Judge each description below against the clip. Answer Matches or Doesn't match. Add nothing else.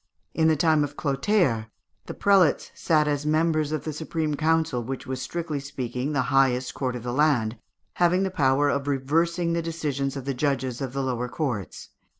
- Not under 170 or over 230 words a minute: Matches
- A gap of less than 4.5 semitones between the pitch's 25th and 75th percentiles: Matches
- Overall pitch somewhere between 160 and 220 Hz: Doesn't match